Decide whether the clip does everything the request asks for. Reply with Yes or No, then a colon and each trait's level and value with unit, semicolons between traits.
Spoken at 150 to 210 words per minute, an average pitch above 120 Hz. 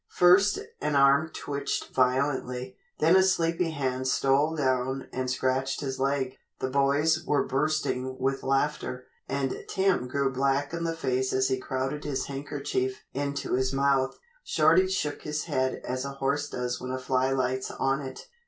Yes: average, 160 wpm; low, 135 Hz